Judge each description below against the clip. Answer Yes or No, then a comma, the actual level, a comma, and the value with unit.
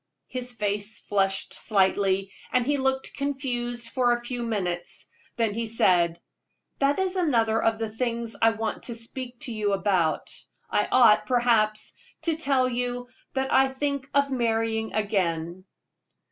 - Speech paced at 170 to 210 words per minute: No, average, 145 wpm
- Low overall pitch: No, high, 230 Hz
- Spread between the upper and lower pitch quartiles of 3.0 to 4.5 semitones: Yes, average, 3.7 semitones